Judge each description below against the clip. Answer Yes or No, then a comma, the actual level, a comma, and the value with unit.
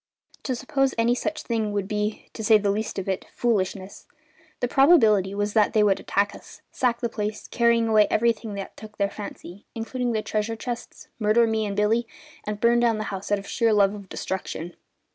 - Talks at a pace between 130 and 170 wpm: No, average, 200 wpm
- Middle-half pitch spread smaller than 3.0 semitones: Yes, narrow, 2.4 semitones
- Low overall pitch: No, high, 215 Hz